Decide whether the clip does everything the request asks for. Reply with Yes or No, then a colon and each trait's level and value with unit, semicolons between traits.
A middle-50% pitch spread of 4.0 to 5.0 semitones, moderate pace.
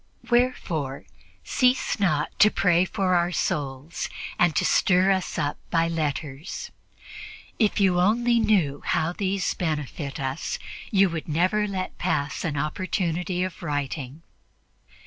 No: average, 4.4 semitones; slow, 125 wpm